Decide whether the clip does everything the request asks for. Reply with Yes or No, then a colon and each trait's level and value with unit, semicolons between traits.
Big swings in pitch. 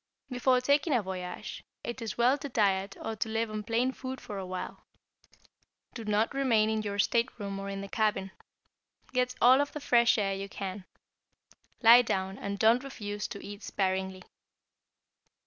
No: average, 3.8 semitones